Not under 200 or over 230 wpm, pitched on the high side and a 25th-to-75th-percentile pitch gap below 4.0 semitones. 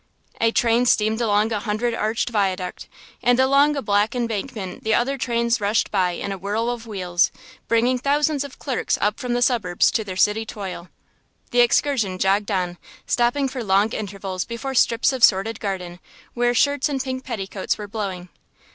No: average, 175 wpm; high, 225 Hz; average, 3.6 semitones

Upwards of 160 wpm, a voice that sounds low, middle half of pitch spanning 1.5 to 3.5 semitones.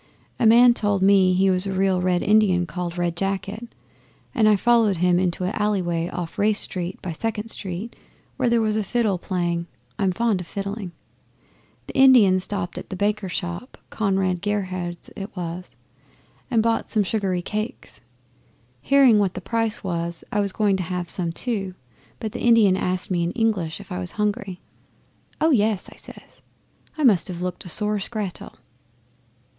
No: average, 175 wpm; high, 195 Hz; average, 3.1 semitones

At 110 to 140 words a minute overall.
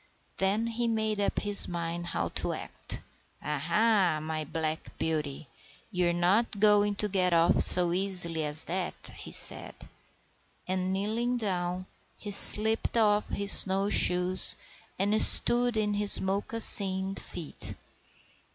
Yes: slow, 135 wpm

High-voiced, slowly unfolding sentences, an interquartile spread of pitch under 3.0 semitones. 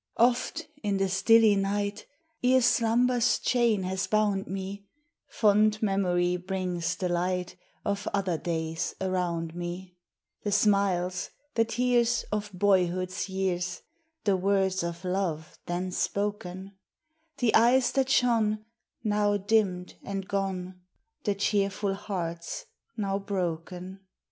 Yes: high, 195 Hz; slow, 115 wpm; narrow, 2.6 semitones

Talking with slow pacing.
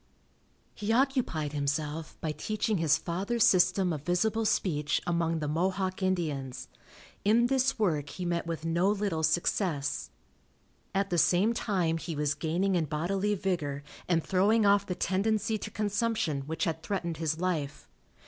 No: average, 150 wpm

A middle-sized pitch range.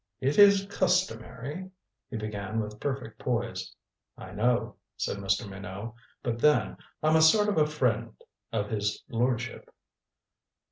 No: wide, 6.1 semitones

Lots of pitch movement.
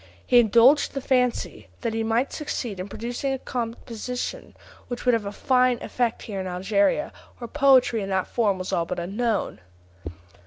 No: average, 3.8 semitones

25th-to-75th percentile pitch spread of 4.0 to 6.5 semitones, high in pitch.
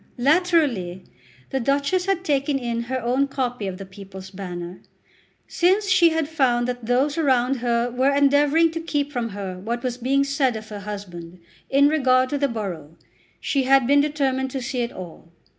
Yes: average, 4.8 semitones; very high, 255 Hz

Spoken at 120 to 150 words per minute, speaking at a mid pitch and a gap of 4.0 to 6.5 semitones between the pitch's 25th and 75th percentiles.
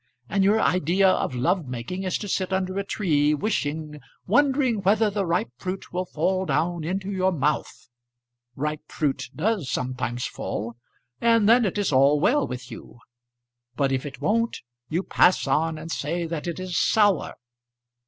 No: average, 165 wpm; medium, 180 Hz; average, 5.0 semitones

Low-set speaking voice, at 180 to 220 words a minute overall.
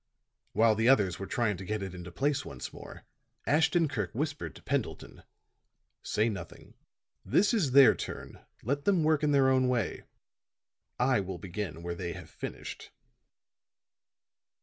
No: low, 115 Hz; average, 150 wpm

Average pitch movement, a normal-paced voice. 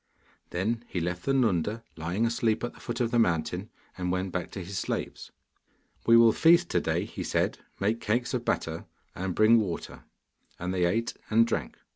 Yes: average, 4.6 semitones; average, 190 wpm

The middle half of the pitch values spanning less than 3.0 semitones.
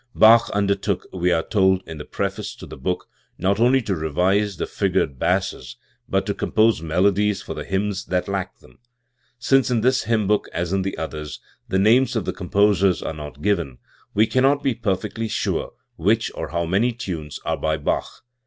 No: average, 3.9 semitones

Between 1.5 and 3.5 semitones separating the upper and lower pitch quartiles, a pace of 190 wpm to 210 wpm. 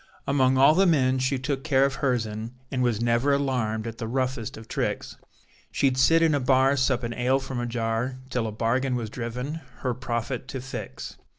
Yes: narrow, 2.4 semitones; average, 200 wpm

